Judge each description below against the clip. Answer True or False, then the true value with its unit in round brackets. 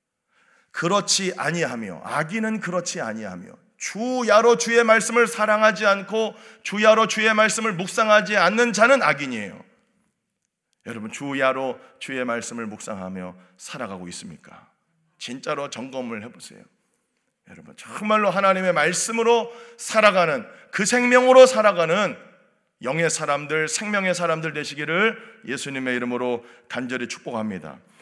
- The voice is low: False (190 Hz)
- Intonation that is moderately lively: False (8.0 semitones)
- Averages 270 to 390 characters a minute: True (305 characters per minute)